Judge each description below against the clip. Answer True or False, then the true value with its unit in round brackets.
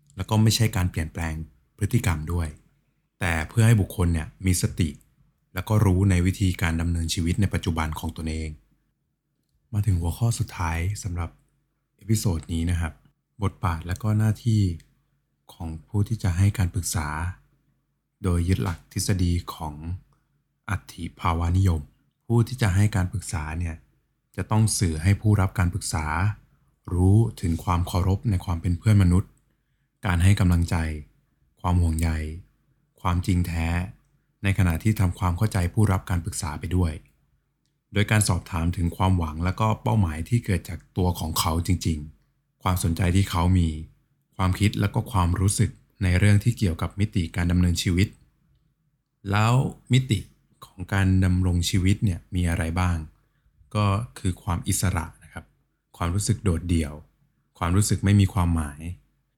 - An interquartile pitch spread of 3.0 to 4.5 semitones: True (4.1 semitones)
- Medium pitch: False (95 Hz)